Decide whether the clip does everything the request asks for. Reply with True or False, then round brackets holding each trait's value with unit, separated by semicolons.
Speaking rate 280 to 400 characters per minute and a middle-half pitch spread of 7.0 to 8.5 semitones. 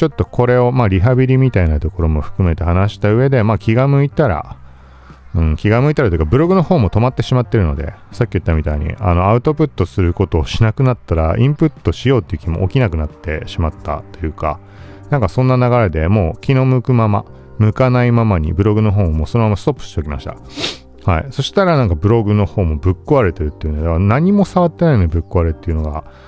False (490 characters per minute; 7.4 semitones)